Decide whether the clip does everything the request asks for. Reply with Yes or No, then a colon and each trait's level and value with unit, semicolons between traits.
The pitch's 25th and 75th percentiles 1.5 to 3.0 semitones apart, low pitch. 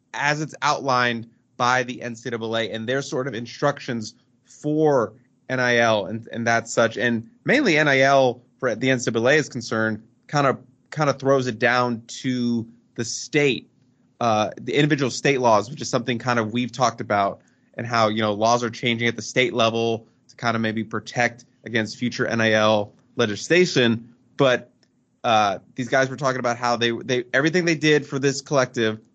Yes: narrow, 2.4 semitones; low, 125 Hz